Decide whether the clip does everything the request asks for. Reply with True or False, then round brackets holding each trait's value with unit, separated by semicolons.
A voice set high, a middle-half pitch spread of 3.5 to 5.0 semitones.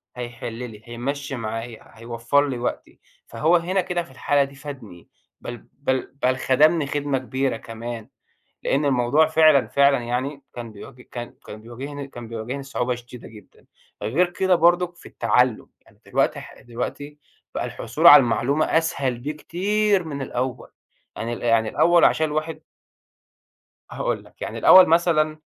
False (135 Hz; 4.4 semitones)